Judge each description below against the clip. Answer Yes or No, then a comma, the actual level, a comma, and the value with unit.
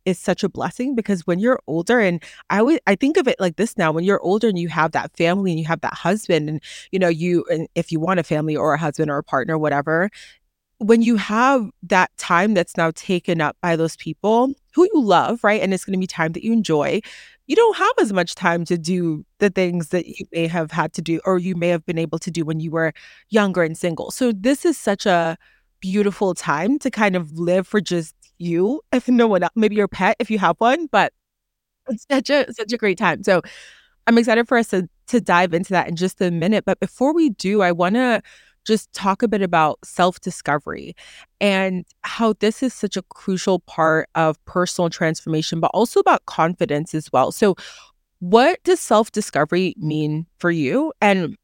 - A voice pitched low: No, medium, 185 Hz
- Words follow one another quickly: Yes, fast, 220 wpm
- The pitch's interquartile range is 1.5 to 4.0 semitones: No, average, 4.8 semitones